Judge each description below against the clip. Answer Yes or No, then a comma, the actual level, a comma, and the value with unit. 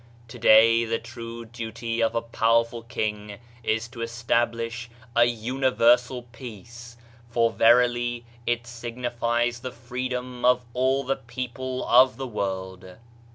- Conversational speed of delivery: No, slow, 120 wpm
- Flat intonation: Yes, narrow, 1.2 semitones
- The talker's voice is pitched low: Yes, low, 120 Hz